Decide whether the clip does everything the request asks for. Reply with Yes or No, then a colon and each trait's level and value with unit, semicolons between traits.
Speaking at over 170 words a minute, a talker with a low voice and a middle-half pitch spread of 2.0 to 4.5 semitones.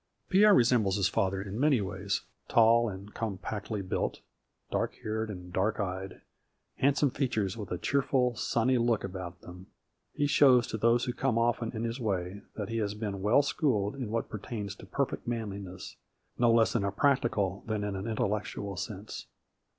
Yes: average, 180 wpm; low, 110 Hz; average, 3.4 semitones